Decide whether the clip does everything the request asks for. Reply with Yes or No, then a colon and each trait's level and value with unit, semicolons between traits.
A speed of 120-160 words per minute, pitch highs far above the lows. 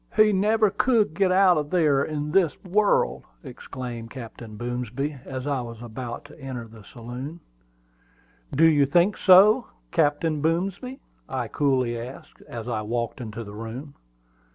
Yes: average, 150 wpm; wide, 6.6 semitones